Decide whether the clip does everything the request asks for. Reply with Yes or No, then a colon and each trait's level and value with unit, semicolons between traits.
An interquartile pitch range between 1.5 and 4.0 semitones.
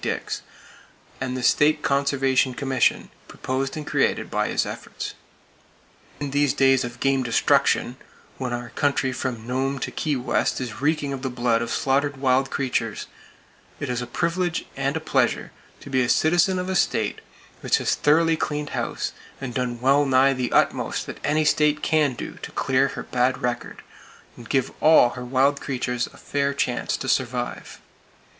Yes: narrow, 2.5 semitones